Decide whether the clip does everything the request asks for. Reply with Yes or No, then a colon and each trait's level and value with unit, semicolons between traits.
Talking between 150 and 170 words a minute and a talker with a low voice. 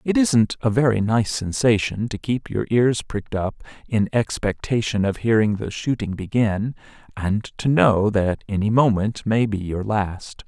Yes: average, 165 wpm; low, 110 Hz